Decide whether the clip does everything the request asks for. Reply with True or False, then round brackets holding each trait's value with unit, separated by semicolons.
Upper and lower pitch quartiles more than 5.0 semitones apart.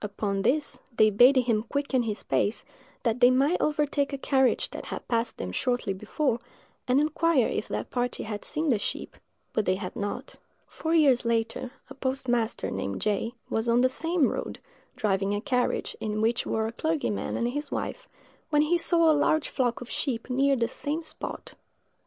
False (4.7 semitones)